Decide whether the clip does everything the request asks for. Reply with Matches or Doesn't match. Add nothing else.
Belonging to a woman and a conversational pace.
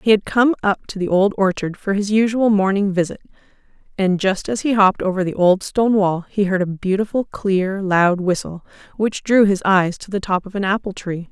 Doesn't match